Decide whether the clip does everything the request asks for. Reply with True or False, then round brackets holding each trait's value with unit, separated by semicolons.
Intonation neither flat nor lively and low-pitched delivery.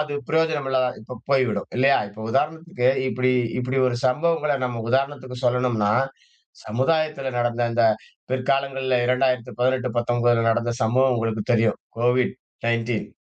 False (2.3 semitones; 125 Hz)